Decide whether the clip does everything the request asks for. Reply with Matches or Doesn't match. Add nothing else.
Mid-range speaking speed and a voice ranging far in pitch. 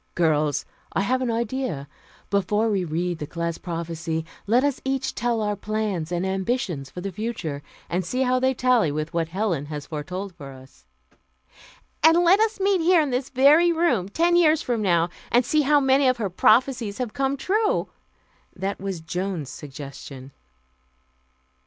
Matches